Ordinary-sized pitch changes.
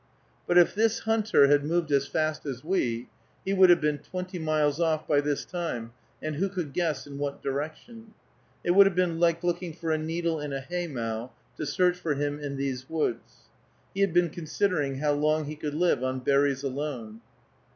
Yes: average, 3.8 semitones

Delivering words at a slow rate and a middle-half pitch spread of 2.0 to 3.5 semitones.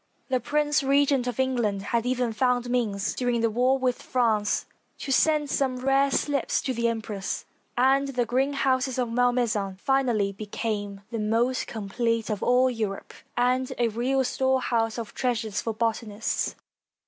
No: average, 155 wpm; average, 2.8 semitones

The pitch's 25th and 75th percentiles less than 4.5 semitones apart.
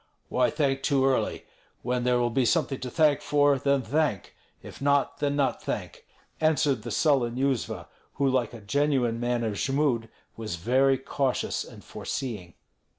Yes: average, 3.0 semitones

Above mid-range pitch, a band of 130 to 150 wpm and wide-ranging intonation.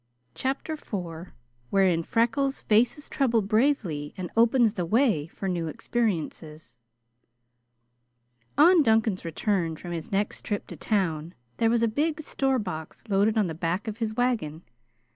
Yes: high, 210 Hz; average, 145 wpm; wide, 5.9 semitones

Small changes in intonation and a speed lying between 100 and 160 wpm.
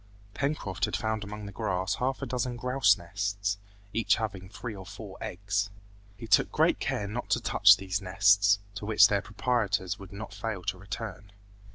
No: narrow, 2.1 semitones; average, 180 wpm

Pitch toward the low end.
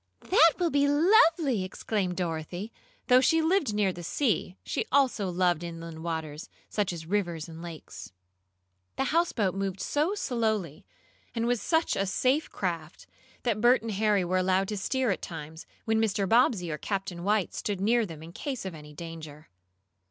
No: high, 195 Hz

